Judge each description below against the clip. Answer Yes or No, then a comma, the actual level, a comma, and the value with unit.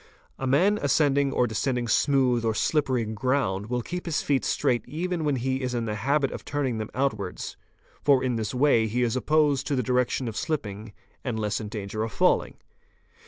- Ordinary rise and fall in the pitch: Yes, average, 4.1 semitones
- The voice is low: Yes, low, 125 Hz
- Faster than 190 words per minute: Yes, average, 200 wpm